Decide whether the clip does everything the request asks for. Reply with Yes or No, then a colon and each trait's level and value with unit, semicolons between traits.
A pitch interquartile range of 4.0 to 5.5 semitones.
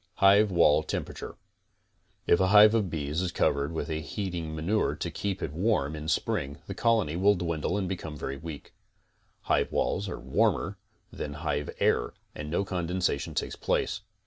Yes: average, 4.5 semitones